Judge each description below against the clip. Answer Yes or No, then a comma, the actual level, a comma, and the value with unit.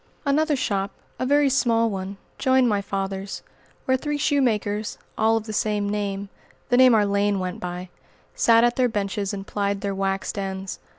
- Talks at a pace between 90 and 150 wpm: No, average, 175 wpm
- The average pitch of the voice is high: Yes, high, 205 Hz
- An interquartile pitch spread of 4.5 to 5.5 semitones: No, average, 3.8 semitones